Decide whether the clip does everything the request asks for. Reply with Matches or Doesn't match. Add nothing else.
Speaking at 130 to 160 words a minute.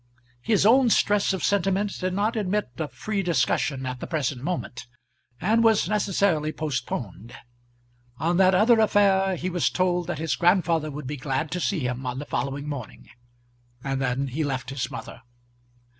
Doesn't match